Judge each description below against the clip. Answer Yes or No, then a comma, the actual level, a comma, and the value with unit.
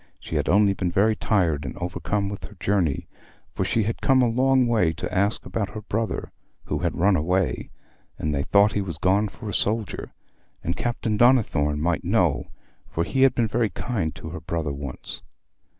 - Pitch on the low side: Yes, low, 100 Hz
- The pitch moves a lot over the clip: No, average, 4.8 semitones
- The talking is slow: No, average, 195 wpm